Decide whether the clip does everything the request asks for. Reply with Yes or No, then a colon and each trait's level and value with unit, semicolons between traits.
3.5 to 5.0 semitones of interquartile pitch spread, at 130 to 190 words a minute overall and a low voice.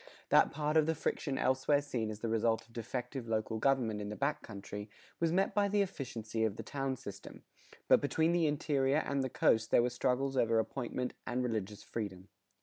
No: average, 4.2 semitones; average, 200 wpm; low, 125 Hz